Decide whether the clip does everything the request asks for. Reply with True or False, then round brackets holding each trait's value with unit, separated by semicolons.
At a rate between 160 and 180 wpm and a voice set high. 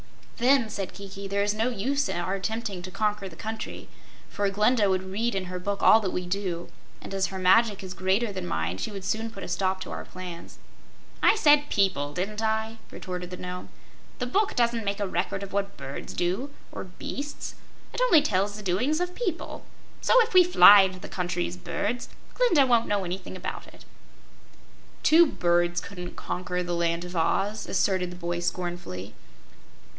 False (190 wpm; 195 Hz)